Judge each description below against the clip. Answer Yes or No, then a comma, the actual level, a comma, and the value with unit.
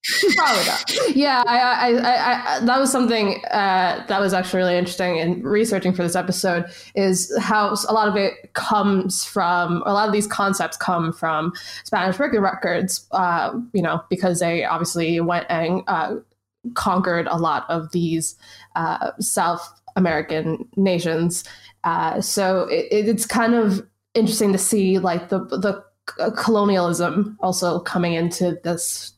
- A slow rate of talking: No, average, 150 wpm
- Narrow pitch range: No, average, 3.8 semitones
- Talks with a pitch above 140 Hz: Yes, high, 190 Hz